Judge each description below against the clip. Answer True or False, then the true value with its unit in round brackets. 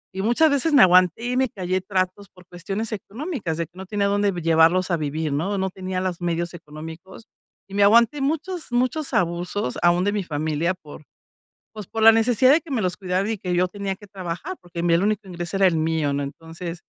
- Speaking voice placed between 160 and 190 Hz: True (185 Hz)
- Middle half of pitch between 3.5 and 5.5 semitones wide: True (3.9 semitones)